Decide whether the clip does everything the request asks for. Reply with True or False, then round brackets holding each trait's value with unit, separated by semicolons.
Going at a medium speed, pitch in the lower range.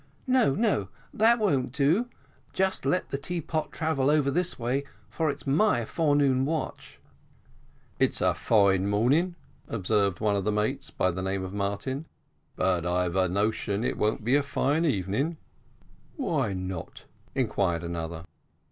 True (150 wpm; 120 Hz)